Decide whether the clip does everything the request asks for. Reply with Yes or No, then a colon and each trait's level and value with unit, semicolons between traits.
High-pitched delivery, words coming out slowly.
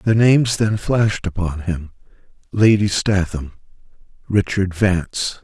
No: low, 100 Hz; slow, 90 wpm